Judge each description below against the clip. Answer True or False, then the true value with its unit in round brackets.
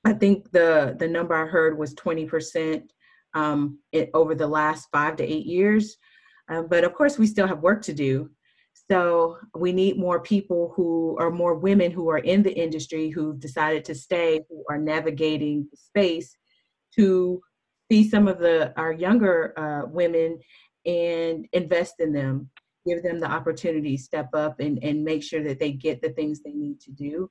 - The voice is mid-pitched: True (165 Hz)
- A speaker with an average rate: True (185 wpm)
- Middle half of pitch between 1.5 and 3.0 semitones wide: True (2.6 semitones)